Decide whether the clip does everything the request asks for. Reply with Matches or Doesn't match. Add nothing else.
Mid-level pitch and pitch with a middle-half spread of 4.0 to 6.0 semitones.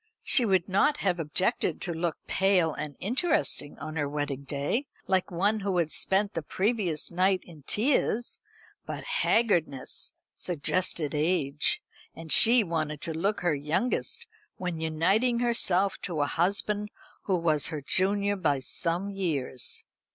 Matches